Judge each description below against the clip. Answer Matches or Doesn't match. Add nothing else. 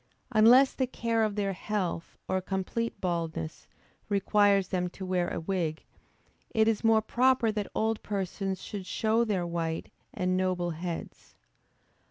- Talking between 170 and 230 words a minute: Doesn't match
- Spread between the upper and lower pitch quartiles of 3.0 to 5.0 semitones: Matches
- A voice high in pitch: Matches